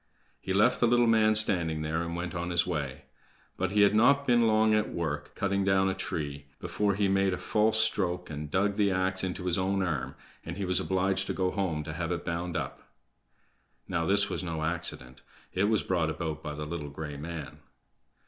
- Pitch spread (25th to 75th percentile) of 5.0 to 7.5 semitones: No, average, 3.8 semitones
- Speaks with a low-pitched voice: Yes, very low, 90 Hz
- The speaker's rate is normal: No, fast, 210 wpm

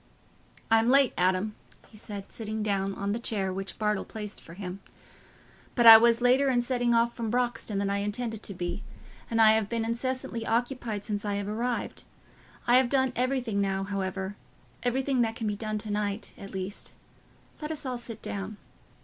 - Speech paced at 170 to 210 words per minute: Yes, average, 180 wpm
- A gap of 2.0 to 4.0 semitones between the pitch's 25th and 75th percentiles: Yes, average, 3.2 semitones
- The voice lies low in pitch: No, high, 220 Hz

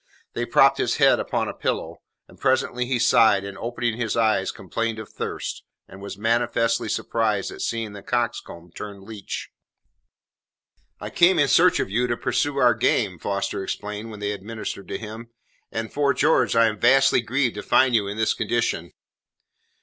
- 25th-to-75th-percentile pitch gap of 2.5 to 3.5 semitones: Yes, average, 2.9 semitones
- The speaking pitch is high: No, low, 115 Hz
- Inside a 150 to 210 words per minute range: Yes, average, 180 wpm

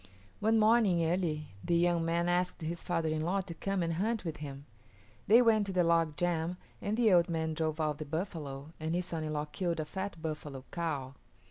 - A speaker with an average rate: No, fast, 215 wpm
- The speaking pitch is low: No, medium, 170 Hz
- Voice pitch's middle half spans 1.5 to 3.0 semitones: Yes, average, 2.7 semitones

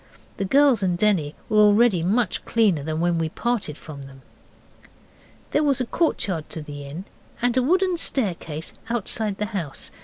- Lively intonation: Yes, wide, 7.0 semitones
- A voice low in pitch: No, high, 200 Hz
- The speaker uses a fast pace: No, average, 165 wpm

